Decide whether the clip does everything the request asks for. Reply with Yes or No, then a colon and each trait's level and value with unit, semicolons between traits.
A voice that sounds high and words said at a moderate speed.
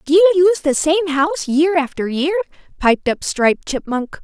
Yes: very high, 300 Hz; average, 185 wpm